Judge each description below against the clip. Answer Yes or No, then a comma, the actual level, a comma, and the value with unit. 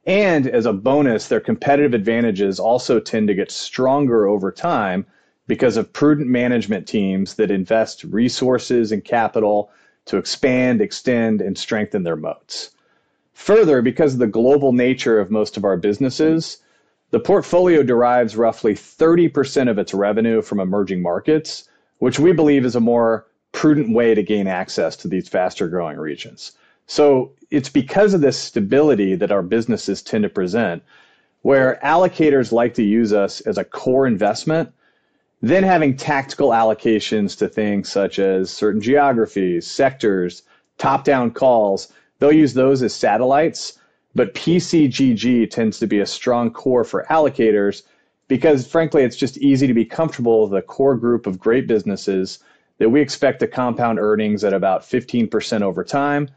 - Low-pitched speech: Yes, low, 120 Hz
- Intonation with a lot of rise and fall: No, average, 4.7 semitones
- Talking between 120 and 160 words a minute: Yes, average, 155 wpm